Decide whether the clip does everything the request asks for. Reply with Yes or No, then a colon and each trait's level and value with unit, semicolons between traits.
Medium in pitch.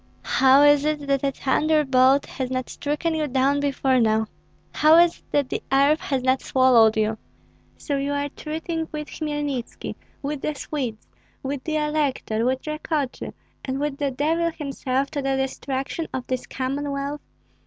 No: very high, 280 Hz